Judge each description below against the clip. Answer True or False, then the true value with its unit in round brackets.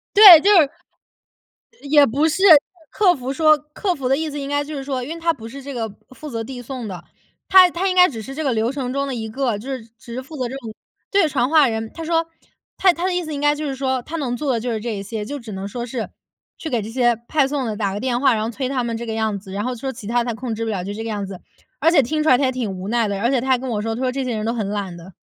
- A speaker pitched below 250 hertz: False (255 Hz)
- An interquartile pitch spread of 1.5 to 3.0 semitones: False (4.4 semitones)